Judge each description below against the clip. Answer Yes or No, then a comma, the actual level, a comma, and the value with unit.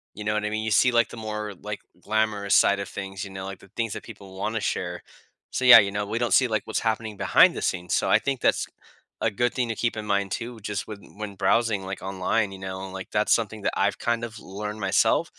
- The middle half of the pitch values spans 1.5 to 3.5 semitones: Yes, narrow, 2.5 semitones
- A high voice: No, low, 105 Hz